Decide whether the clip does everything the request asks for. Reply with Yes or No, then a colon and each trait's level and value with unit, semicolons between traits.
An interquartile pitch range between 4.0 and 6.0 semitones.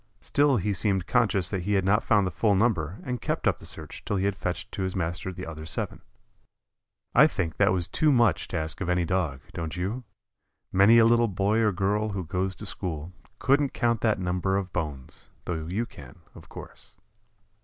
No: average, 3.5 semitones